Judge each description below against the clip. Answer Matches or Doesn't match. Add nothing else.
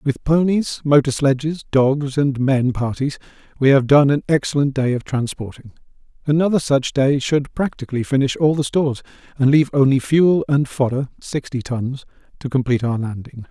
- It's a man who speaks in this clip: Matches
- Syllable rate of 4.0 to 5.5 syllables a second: Matches